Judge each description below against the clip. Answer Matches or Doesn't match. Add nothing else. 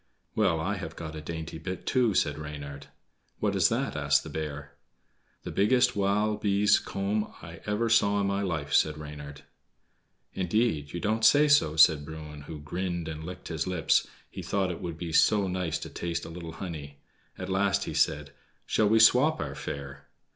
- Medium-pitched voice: Doesn't match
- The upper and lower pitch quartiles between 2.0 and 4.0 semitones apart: Doesn't match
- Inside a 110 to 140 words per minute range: Doesn't match